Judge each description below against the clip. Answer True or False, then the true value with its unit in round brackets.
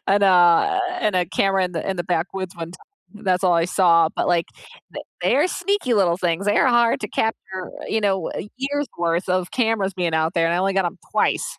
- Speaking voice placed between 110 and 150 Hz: False (185 Hz)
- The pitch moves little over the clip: False (3.2 semitones)